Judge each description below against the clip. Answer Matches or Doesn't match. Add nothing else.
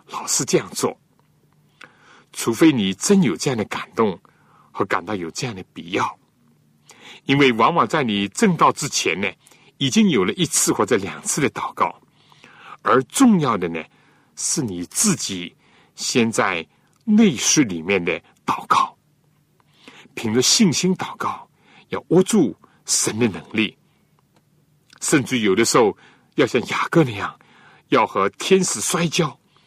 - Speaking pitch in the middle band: Matches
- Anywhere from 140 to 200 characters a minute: Matches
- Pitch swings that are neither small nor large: Doesn't match